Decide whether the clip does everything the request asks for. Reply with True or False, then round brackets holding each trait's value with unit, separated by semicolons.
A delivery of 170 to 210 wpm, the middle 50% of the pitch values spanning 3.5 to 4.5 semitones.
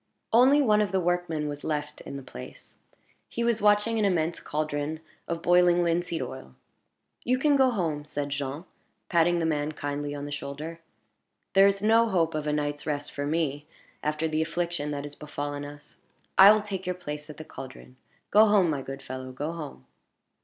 True (190 wpm; 3.9 semitones)